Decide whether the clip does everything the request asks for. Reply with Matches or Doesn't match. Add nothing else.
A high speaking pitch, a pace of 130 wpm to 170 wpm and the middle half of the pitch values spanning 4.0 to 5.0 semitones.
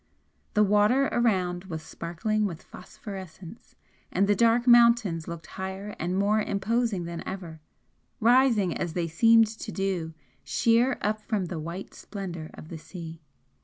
Matches